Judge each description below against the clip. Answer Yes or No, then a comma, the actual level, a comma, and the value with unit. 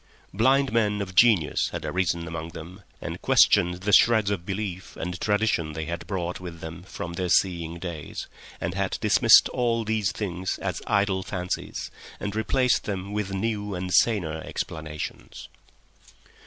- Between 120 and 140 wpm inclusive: No, average, 155 wpm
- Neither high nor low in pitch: No, very low, 95 Hz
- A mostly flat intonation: No, average, 3.5 semitones